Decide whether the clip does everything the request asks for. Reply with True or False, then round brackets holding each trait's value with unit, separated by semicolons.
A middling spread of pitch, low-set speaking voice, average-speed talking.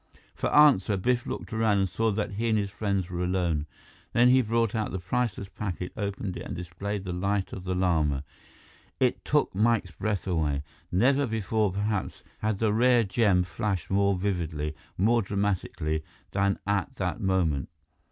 True (3.2 semitones; 100 Hz; 170 wpm)